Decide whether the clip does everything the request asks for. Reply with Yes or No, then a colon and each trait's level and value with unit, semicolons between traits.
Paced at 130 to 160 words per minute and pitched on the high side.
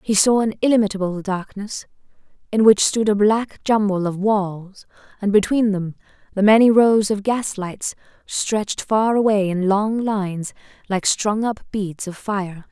Yes: average, 155 wpm; high, 205 Hz